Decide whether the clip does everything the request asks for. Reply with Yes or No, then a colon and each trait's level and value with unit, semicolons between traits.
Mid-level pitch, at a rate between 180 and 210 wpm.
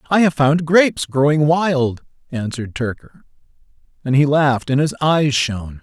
No: medium, 145 Hz; average, 155 wpm